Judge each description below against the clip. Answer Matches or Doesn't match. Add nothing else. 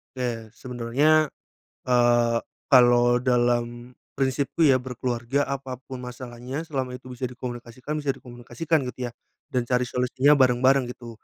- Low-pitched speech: Matches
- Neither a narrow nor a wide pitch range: Doesn't match